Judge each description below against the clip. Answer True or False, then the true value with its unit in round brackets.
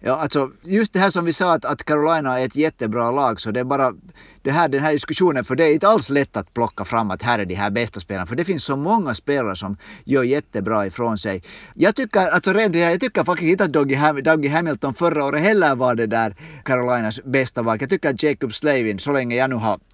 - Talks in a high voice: False (140 Hz)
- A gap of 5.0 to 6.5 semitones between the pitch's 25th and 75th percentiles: True (5.6 semitones)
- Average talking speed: False (245 wpm)